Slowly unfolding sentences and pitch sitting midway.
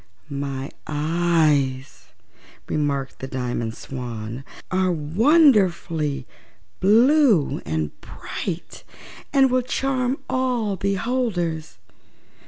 Yes: slow, 75 wpm; medium, 170 Hz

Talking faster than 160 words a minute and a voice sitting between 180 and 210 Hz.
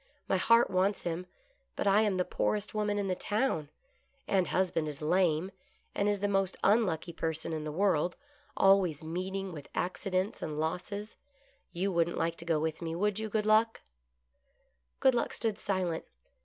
Yes: average, 180 wpm; medium, 185 Hz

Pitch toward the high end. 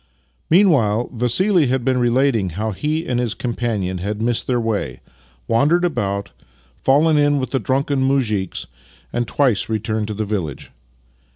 No: low, 120 Hz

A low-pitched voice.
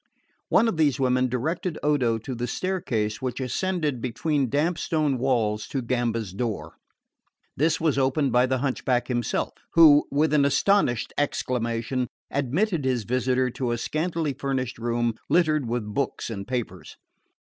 Yes: low, 130 Hz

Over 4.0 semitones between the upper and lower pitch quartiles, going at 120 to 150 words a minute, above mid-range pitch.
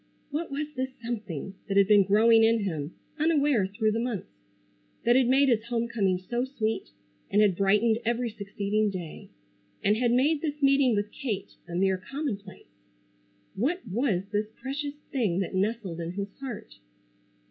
No: average, 4.6 semitones; average, 160 wpm; high, 220 Hz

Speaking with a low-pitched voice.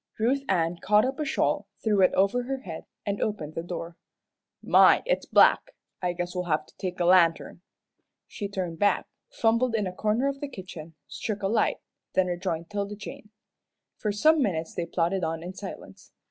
No: high, 190 Hz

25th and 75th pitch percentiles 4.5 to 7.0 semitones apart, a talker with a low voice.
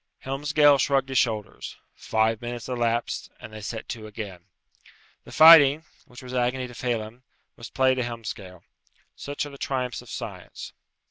No: average, 3.2 semitones; low, 125 Hz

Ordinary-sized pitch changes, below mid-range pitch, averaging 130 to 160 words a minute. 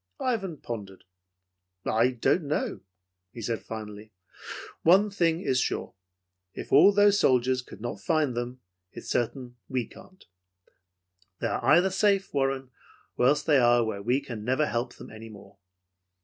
No: wide, 5.7 semitones; low, 130 Hz; average, 155 wpm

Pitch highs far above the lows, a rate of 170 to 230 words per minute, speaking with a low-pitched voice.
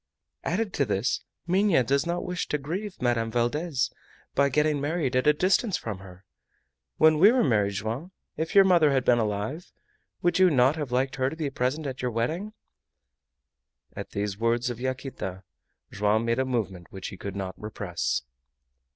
Yes: wide, 6.3 semitones; average, 175 wpm; low, 130 Hz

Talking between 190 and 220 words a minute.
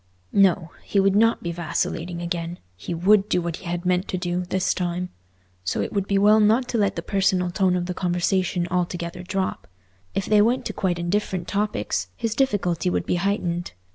Yes: average, 195 wpm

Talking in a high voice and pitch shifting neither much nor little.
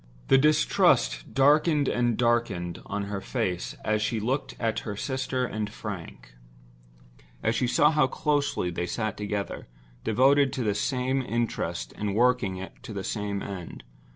No: low, 115 Hz; average, 4.7 semitones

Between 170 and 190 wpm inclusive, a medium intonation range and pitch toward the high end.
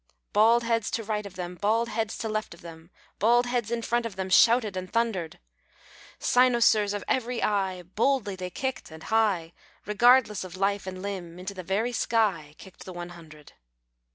Yes: average, 180 wpm; average, 4.0 semitones; high, 205 Hz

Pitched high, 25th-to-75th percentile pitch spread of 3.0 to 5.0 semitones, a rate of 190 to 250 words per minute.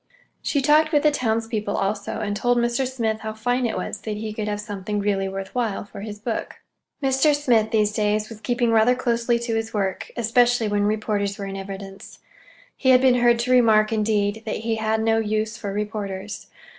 No: high, 220 Hz; narrow, 2.4 semitones; average, 200 wpm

